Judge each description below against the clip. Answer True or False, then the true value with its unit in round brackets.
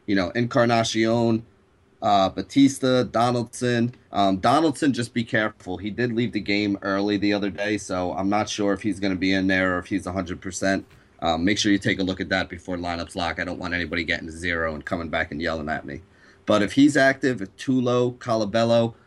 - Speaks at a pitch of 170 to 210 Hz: False (100 Hz)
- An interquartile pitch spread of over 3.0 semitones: True (3.7 semitones)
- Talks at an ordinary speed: False (210 wpm)